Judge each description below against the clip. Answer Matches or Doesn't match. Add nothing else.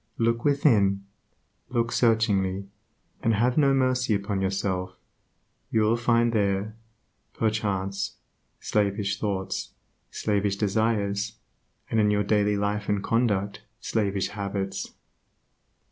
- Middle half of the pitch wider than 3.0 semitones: Doesn't match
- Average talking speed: Doesn't match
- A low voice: Matches